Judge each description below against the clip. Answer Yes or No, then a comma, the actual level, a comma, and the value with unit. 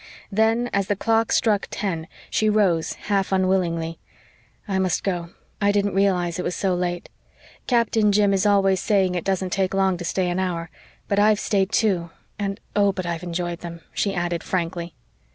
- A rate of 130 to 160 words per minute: No, average, 180 wpm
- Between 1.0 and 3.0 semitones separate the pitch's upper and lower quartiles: Yes, narrow, 2.6 semitones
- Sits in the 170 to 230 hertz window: Yes, high, 190 Hz